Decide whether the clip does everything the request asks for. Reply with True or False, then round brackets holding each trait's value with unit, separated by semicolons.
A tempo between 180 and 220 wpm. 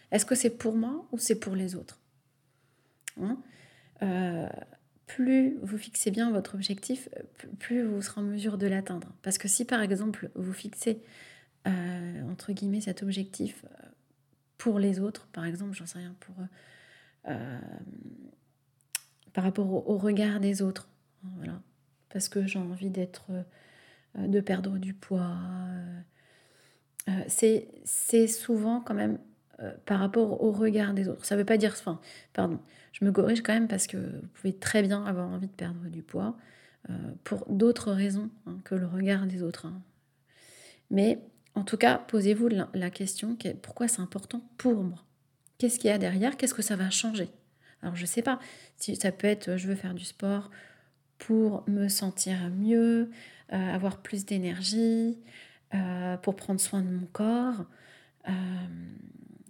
False (165 wpm)